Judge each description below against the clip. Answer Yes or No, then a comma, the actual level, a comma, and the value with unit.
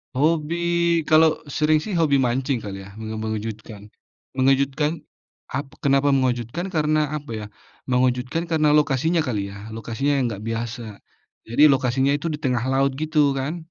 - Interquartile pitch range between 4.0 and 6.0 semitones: Yes, average, 4.5 semitones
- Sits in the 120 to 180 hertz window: Yes, low, 135 Hz